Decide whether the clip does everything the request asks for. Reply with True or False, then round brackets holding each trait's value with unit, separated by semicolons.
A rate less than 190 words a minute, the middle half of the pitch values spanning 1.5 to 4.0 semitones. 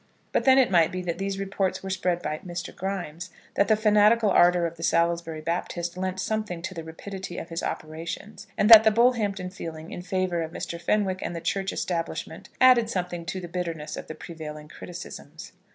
False (200 wpm; 2.8 semitones)